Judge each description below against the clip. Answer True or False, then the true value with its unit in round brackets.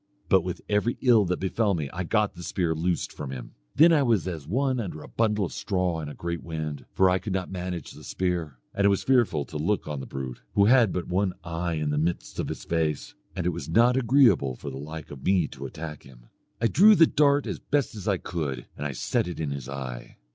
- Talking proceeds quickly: True (245 wpm)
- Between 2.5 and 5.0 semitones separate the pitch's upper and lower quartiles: False (5.6 semitones)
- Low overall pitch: True (90 Hz)